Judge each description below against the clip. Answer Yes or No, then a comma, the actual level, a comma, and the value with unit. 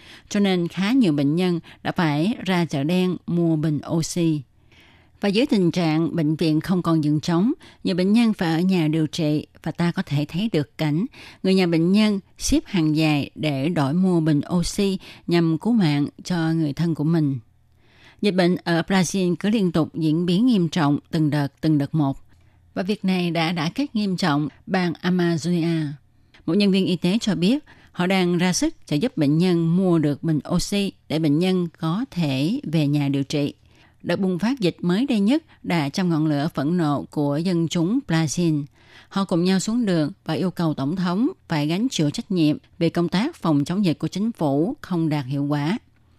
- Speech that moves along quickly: No, average, 205 wpm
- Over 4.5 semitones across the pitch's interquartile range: No, average, 3.6 semitones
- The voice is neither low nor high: Yes, medium, 165 Hz